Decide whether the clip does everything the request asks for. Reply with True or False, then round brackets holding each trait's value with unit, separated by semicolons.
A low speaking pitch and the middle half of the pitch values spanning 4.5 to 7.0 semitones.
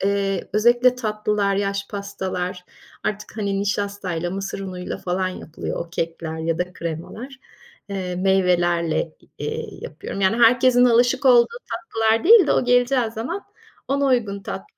False (200 Hz; 4.8 semitones)